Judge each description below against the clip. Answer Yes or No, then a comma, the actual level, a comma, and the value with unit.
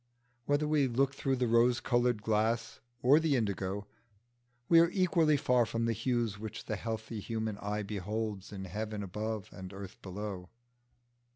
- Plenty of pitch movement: No, average, 3.5 semitones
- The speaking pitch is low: Yes, low, 110 Hz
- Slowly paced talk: No, average, 160 wpm